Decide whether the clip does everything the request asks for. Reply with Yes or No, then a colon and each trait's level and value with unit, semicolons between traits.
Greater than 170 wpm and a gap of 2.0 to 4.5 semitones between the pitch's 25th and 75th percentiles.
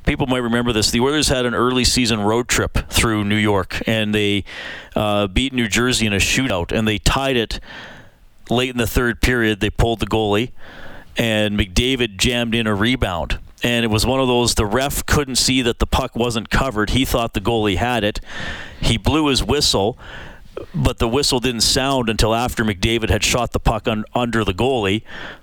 Yes: average, 200 wpm; average, 2.8 semitones